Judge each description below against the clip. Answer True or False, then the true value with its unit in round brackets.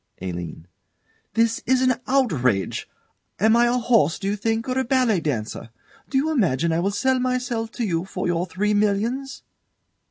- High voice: True (220 Hz)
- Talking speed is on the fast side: False (170 wpm)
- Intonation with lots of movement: True (6.8 semitones)